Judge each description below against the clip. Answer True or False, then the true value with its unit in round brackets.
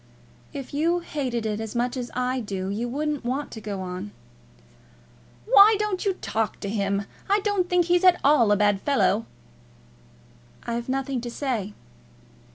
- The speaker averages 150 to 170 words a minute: True (165 wpm)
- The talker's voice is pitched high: True (250 Hz)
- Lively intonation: True (6.2 semitones)